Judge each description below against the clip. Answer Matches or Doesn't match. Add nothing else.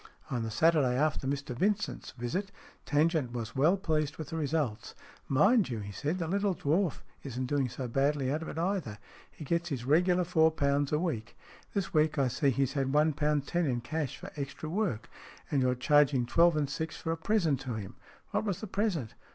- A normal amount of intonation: Matches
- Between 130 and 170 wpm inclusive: Doesn't match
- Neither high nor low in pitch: Matches